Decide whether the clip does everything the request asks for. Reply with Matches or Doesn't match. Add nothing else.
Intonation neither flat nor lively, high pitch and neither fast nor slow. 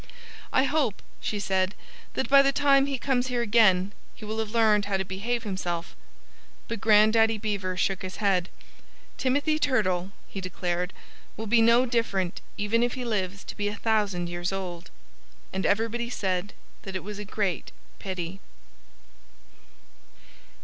Matches